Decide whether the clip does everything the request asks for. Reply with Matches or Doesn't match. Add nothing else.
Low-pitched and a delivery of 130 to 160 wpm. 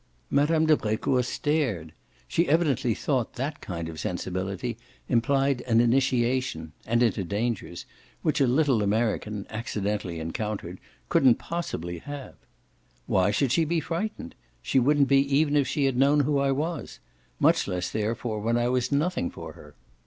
Matches